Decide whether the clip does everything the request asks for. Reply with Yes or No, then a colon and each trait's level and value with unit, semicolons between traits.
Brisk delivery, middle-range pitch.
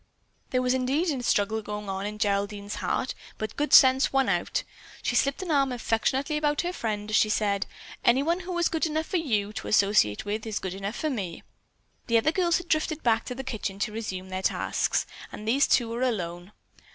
No: fast, 210 wpm; high, 230 Hz